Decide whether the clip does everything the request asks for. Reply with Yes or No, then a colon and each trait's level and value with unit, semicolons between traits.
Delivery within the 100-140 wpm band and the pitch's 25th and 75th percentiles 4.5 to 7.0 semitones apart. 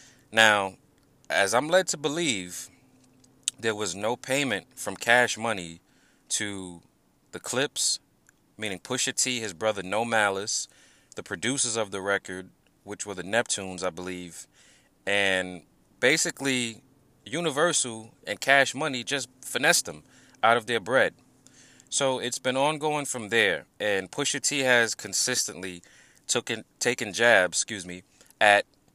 Yes: slow, 135 wpm; average, 5.1 semitones